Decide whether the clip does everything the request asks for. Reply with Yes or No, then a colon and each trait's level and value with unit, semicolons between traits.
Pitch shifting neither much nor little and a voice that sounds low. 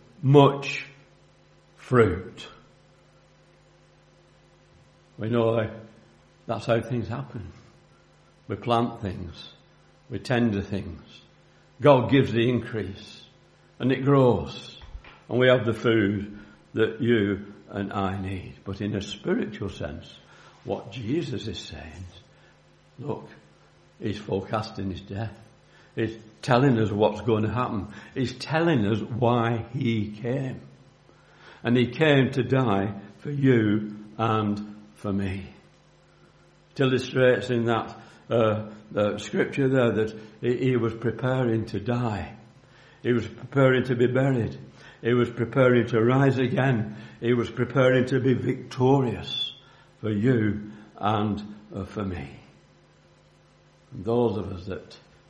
Yes: average, 3.4 semitones; low, 115 Hz